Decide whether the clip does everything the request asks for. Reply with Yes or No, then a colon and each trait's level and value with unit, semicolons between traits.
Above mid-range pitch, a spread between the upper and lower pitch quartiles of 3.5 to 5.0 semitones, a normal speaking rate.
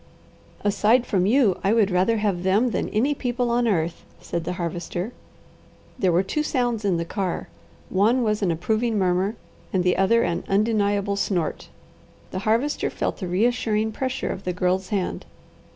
Yes: high, 205 Hz; average, 3.9 semitones; average, 170 wpm